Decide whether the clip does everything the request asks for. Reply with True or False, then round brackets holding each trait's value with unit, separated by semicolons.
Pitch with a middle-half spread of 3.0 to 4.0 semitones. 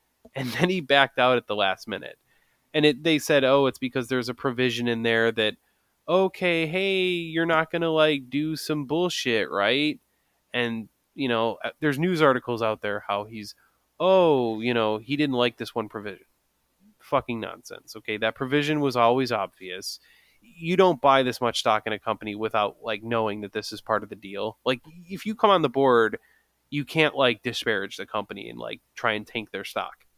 False (5.6 semitones)